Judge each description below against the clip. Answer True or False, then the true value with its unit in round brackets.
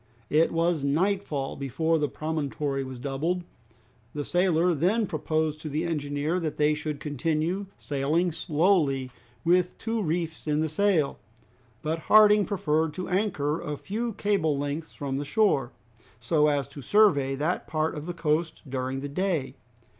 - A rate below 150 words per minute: False (155 wpm)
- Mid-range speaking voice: True (155 Hz)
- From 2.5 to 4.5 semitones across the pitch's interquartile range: True (3.7 semitones)